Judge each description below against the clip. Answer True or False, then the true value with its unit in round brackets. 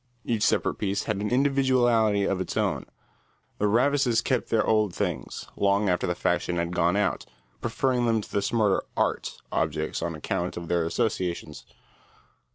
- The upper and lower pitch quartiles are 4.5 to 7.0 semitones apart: True (4.8 semitones)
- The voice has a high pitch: False (105 Hz)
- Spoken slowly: False (165 wpm)